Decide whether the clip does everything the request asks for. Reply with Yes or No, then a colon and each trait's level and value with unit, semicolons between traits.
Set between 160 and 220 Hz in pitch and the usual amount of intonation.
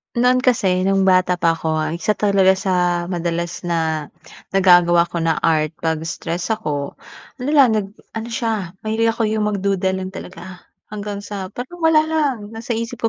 Yes: high, 190 Hz; average, 4.4 semitones